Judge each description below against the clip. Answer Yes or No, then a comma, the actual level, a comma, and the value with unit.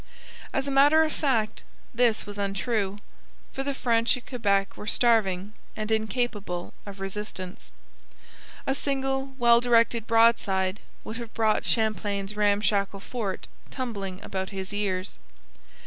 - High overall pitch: Yes, high, 215 Hz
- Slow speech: Yes, slow, 130 wpm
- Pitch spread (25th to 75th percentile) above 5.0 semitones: No, average, 3.5 semitones